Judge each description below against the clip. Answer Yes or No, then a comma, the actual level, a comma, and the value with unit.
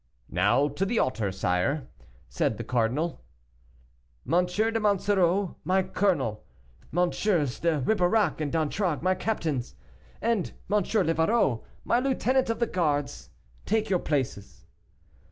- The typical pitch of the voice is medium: Yes, medium, 175 Hz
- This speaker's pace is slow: Yes, slow, 120 wpm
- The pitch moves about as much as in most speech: No, wide, 6.4 semitones